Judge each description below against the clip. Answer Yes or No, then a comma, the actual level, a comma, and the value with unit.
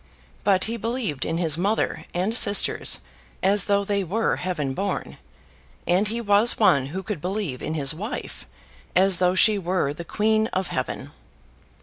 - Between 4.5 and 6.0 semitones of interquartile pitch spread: No, average, 3.5 semitones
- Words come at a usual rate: Yes, average, 160 wpm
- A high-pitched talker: Yes, high, 195 Hz